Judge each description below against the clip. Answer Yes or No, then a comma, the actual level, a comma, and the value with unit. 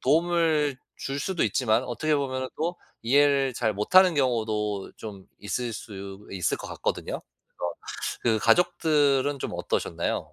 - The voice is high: No, low, 130 Hz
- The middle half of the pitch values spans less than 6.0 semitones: Yes, wide, 5.6 semitones